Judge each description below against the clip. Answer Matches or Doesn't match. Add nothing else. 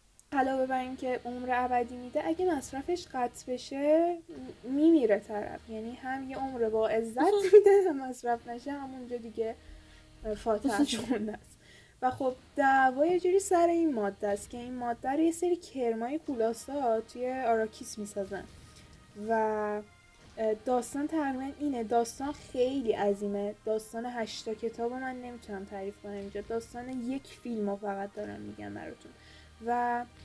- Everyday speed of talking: Matches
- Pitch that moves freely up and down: Doesn't match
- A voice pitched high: Matches